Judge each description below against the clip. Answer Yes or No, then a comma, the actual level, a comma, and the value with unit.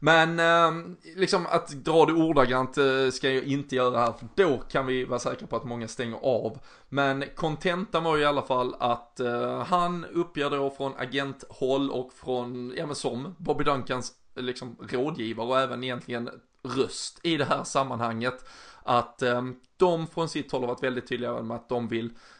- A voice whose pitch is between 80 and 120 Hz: No, low, 130 Hz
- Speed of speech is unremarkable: Yes, average, 180 wpm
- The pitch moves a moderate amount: Yes, average, 4.0 semitones